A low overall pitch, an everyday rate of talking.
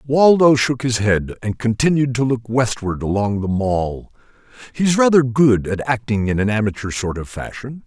Yes: low, 120 Hz; average, 175 wpm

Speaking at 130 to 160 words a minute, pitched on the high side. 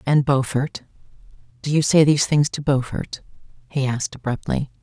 No: slow, 135 wpm; medium, 140 Hz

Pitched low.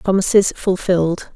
No: medium, 185 Hz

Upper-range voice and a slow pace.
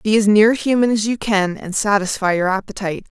No: high, 205 Hz; fast, 205 wpm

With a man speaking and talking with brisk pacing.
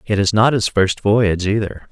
Yes: male; fast, 220 wpm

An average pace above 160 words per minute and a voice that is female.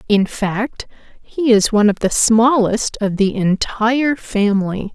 No: average, 145 wpm; female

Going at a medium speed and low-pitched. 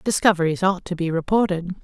No: average, 165 wpm; medium, 180 Hz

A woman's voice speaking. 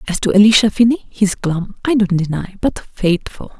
Yes: female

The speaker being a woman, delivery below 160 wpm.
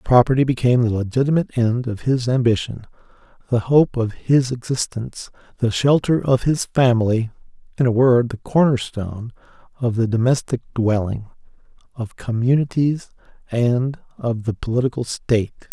No: male; slow, 135 wpm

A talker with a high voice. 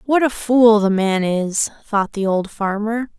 Yes: high, 215 Hz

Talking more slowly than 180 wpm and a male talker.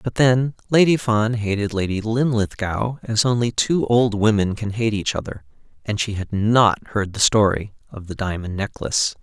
Yes: average, 170 wpm; male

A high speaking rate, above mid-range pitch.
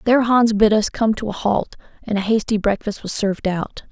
Yes: fast, 230 wpm; high, 215 Hz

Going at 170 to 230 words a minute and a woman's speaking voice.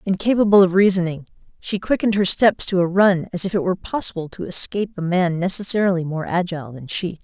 Yes: average, 200 wpm; female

